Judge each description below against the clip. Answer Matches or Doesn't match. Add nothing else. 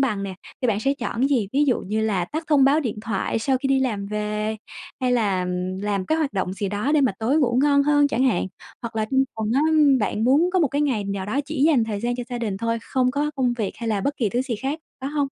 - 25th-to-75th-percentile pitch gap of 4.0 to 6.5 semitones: Matches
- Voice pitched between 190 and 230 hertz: Doesn't match